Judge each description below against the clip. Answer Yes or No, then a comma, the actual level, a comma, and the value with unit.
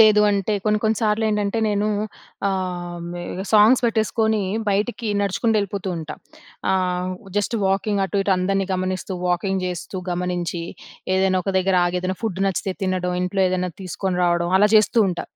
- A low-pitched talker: No, high, 190 Hz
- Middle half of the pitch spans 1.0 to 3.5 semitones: Yes, narrow, 2.5 semitones